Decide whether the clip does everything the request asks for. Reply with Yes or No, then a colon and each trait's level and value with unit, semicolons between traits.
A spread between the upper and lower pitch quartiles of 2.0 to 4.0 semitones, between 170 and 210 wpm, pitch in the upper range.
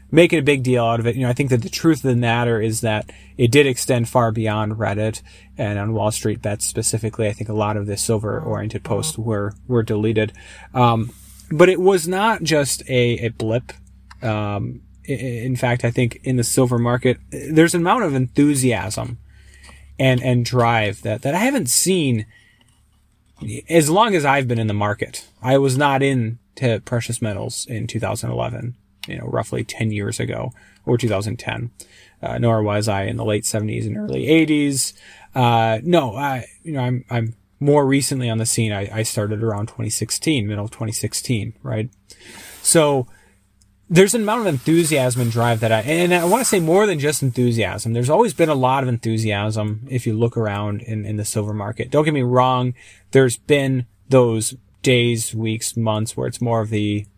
No: average, 3.6 semitones; average, 190 wpm; low, 115 Hz